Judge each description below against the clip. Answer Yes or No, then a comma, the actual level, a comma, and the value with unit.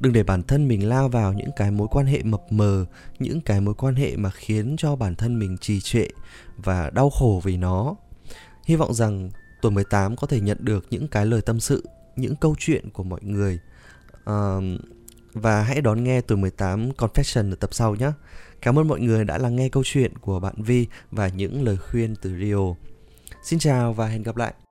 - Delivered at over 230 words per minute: No, average, 215 wpm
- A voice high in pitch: No, low, 110 Hz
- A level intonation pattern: No, average, 4.3 semitones